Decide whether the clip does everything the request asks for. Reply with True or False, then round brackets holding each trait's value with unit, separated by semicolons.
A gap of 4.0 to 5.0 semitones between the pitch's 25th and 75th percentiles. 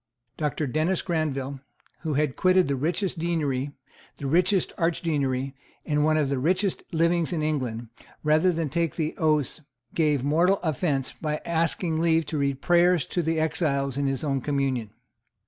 False (3.3 semitones)